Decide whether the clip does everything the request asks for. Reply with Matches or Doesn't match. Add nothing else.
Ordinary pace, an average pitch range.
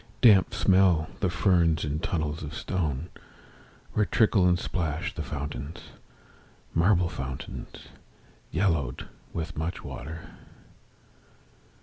Doesn't match